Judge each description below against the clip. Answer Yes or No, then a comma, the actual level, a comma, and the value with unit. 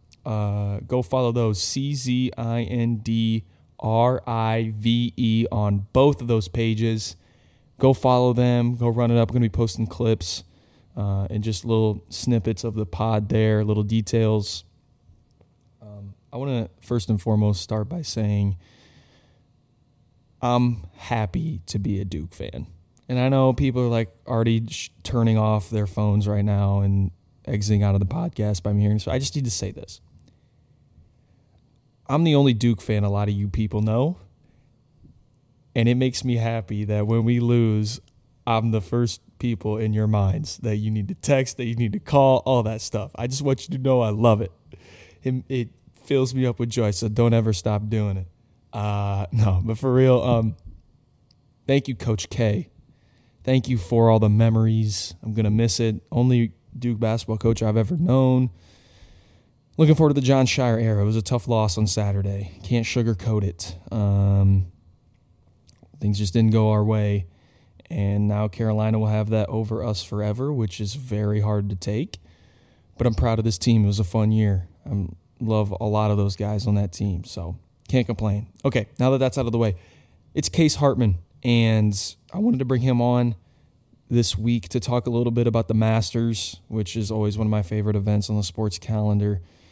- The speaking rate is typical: Yes, average, 185 wpm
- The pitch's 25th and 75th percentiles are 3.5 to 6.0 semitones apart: No, average, 2.7 semitones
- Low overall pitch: Yes, low, 110 Hz